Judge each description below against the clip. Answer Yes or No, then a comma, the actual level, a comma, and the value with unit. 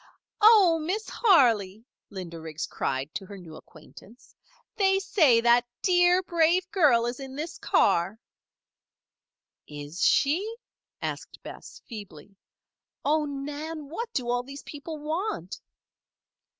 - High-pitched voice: Yes, very high, 275 Hz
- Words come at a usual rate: No, slow, 120 wpm